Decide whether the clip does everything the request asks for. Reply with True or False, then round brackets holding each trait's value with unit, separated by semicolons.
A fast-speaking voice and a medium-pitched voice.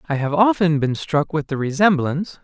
False (195 wpm; 160 Hz)